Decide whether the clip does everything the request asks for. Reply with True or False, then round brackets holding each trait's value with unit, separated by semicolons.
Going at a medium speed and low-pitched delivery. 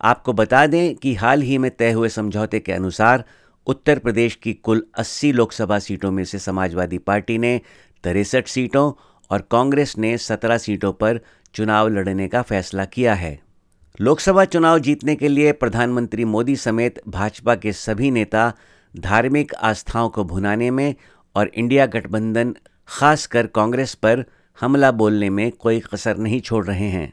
True (155 wpm; 115 Hz)